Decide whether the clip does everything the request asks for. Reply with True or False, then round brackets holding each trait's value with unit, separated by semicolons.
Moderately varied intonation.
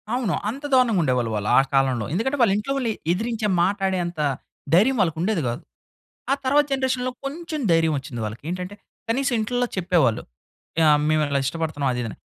False (8.8 semitones)